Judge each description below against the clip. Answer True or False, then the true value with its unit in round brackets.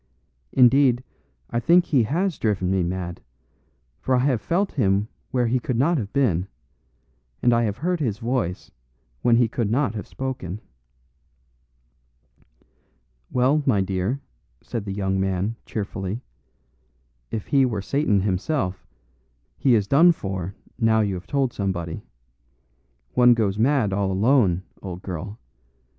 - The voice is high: False (110 Hz)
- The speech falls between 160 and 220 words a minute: False (140 wpm)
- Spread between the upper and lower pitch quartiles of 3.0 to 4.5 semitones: False (5.2 semitones)